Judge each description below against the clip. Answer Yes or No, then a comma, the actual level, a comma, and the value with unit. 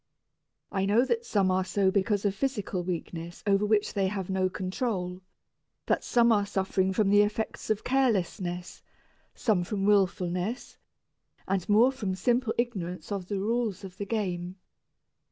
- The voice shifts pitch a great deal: No, average, 2.7 semitones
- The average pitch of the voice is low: No, high, 200 Hz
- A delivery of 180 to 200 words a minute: No, average, 155 wpm